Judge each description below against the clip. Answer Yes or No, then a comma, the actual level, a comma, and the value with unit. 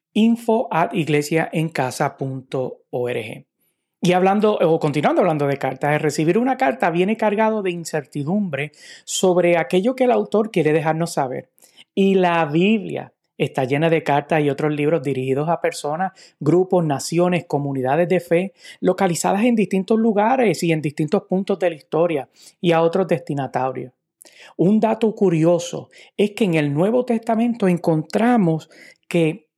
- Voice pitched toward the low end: No, medium, 170 Hz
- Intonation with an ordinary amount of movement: Yes, average, 4.4 semitones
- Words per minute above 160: No, average, 140 wpm